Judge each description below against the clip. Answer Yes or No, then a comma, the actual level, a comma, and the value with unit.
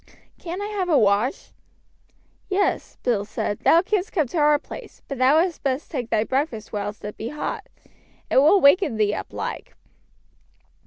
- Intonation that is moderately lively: No, wide, 7.8 semitones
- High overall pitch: Yes, very high, 280 Hz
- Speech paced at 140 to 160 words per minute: No, average, 170 wpm